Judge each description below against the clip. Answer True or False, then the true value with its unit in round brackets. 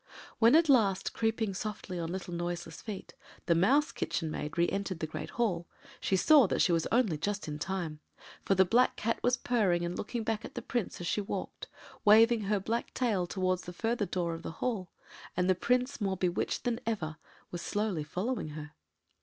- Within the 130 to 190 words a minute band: False (200 wpm)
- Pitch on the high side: True (195 Hz)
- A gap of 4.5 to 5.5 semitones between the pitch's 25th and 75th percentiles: True (4.8 semitones)